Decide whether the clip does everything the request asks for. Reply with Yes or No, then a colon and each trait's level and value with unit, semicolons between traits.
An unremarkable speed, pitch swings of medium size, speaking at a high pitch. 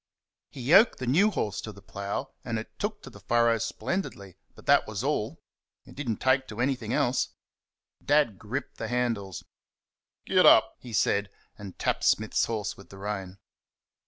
No: average, 175 wpm; average, 4.6 semitones; low, 115 Hz